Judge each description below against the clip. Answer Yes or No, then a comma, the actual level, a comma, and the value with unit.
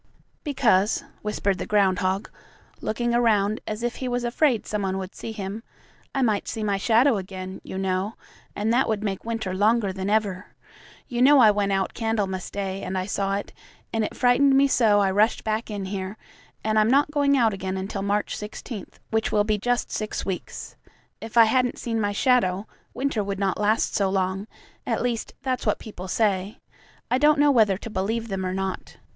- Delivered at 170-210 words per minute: Yes, average, 195 wpm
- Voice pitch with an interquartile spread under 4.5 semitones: Yes, average, 3.2 semitones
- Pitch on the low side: No, high, 210 Hz